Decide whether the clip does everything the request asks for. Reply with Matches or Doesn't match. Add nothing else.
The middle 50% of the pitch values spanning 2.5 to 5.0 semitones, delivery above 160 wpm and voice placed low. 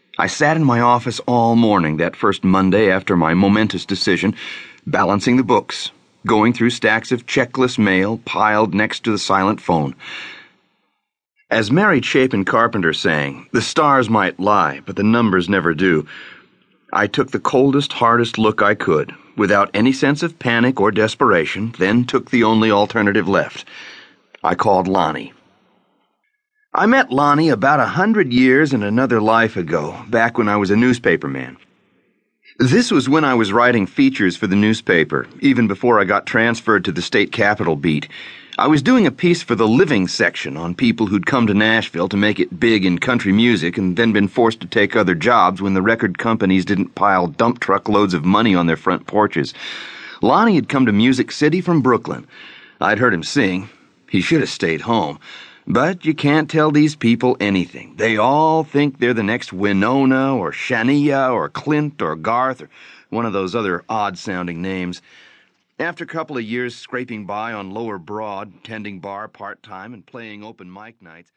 Matches